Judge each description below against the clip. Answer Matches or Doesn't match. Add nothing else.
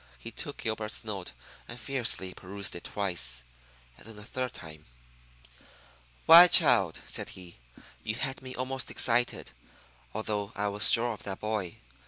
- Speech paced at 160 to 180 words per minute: Doesn't match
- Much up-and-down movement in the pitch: Doesn't match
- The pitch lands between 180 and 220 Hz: Doesn't match